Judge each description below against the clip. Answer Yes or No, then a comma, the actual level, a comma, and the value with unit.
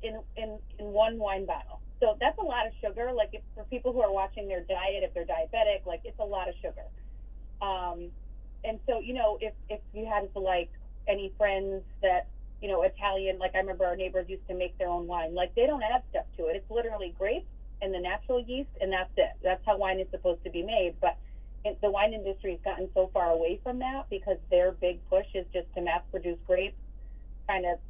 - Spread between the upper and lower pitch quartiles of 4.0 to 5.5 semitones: No, average, 3.0 semitones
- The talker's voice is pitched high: Yes, high, 195 Hz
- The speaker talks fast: Yes, fast, 230 wpm